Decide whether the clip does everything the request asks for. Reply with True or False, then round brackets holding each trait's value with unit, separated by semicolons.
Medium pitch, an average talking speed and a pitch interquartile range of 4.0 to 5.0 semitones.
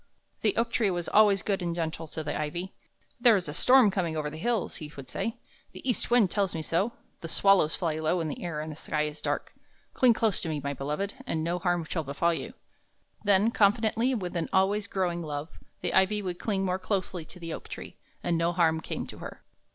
False (175 Hz; 230 wpm; 4.3 semitones)